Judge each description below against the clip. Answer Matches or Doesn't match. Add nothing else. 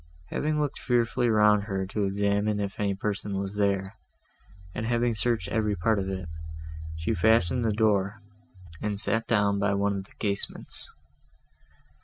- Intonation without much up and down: Matches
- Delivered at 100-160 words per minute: Matches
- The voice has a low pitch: Matches